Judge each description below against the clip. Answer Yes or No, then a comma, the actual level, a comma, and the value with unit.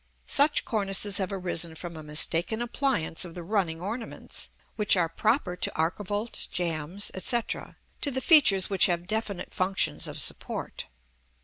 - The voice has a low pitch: No, high, 190 Hz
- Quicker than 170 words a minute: No, average, 145 wpm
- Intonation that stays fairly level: No, average, 4.3 semitones